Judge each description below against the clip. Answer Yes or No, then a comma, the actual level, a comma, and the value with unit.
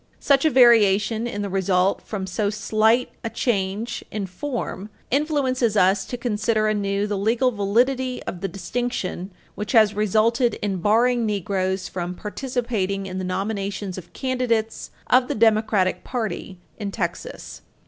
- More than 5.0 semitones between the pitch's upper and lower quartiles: No, average, 3.6 semitones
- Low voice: No, high, 215 Hz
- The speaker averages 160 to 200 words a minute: No, average, 145 wpm